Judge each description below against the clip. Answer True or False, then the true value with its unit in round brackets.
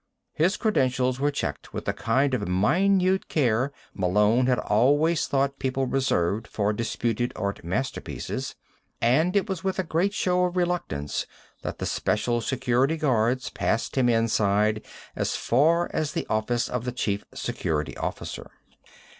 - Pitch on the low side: True (125 Hz)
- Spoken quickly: False (145 wpm)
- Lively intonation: True (6.4 semitones)